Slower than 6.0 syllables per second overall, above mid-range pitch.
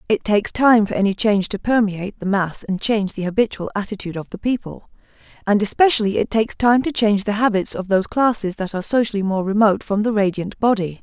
No: 6.4 syllables/s; high, 210 Hz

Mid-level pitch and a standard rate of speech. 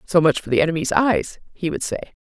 No: medium, 175 Hz; fast, 245 wpm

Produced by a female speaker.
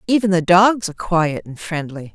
Yes: female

